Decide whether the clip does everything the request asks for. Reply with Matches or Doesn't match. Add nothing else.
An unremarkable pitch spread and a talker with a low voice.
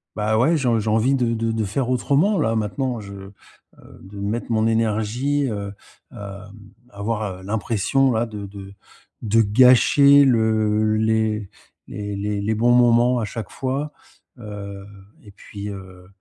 Matches